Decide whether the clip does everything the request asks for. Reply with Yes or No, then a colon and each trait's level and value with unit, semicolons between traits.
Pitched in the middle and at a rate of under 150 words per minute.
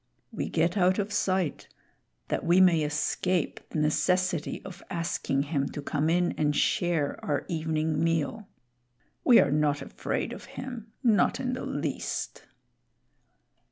Yes: medium, 170 Hz; average, 140 wpm